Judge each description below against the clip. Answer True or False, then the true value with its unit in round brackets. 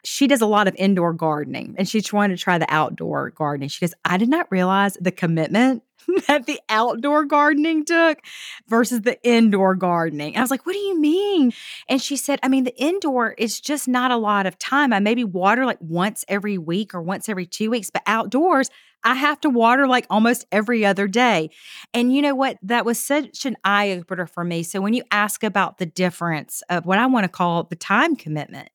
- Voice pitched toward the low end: False (220 Hz)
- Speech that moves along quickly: True (220 wpm)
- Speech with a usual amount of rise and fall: False (6.0 semitones)